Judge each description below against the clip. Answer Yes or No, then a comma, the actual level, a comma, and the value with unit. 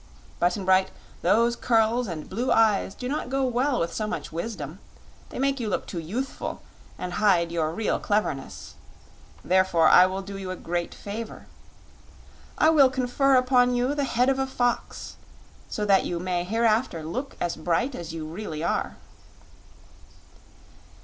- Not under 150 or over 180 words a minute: Yes, average, 160 wpm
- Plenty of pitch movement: Yes, wide, 6.0 semitones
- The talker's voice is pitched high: Yes, high, 210 Hz